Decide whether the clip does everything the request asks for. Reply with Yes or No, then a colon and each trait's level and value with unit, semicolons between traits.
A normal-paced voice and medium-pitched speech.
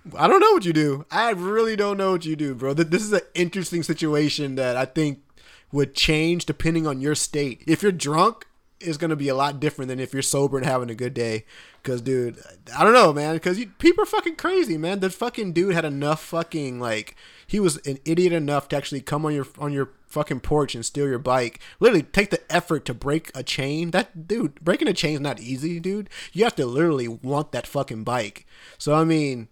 No: fast, 230 wpm; medium, 150 Hz